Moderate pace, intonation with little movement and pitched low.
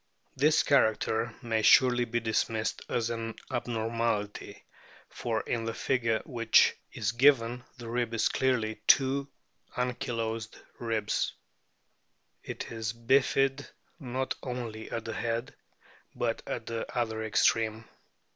No: slow, 120 wpm; narrow, 1.8 semitones; low, 115 Hz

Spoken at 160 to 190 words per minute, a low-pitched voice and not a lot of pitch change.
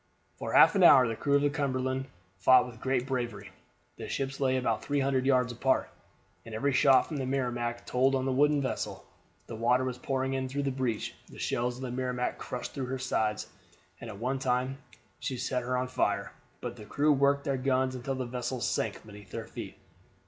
No: fast, 205 wpm; low, 130 Hz; narrow, 1.7 semitones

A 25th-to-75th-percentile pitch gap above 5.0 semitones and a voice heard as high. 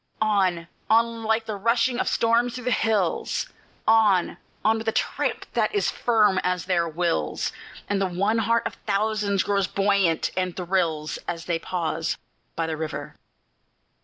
No: average, 4.2 semitones; high, 200 Hz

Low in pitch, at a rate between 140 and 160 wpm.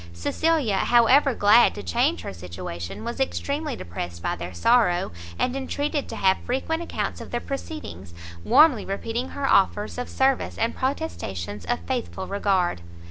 No: high, 230 Hz; average, 150 wpm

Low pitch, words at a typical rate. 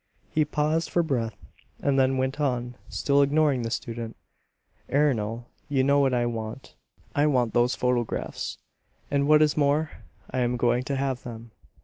Yes: low, 130 Hz; average, 160 wpm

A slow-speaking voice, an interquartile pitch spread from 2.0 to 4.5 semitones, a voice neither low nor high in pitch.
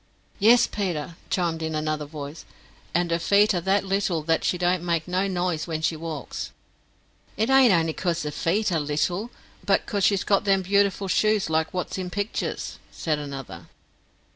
No: average, 175 wpm; average, 3.7 semitones; medium, 175 Hz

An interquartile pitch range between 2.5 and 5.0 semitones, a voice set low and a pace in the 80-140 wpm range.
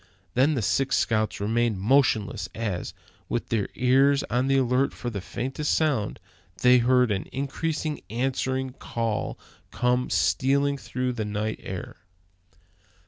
Yes: average, 3.7 semitones; low, 125 Hz; slow, 135 wpm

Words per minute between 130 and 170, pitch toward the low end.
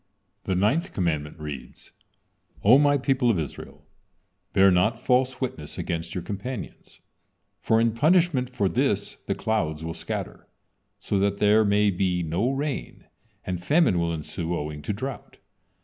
Yes: average, 150 wpm; low, 100 Hz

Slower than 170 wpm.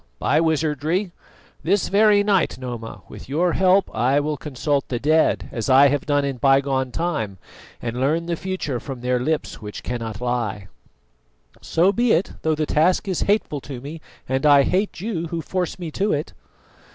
No: average, 175 wpm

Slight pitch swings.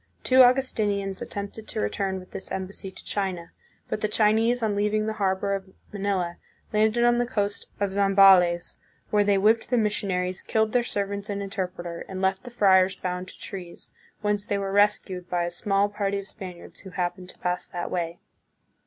Yes: narrow, 2.2 semitones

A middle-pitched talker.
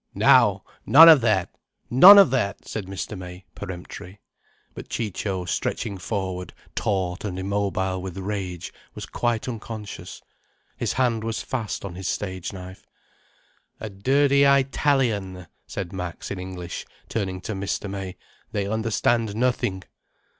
No: low, 100 Hz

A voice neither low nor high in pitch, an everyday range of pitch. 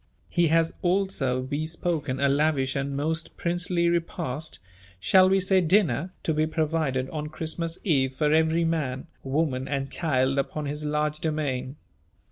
Yes: medium, 155 Hz; average, 3.2 semitones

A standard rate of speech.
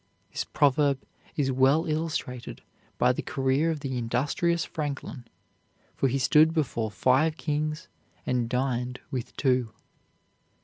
No: slow, 125 wpm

